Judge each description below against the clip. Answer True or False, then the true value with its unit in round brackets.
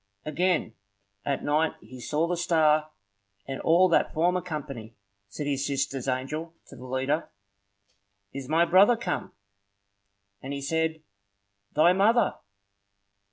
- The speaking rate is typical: False (125 wpm)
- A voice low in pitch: False (155 Hz)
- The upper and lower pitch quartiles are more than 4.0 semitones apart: False (3.7 semitones)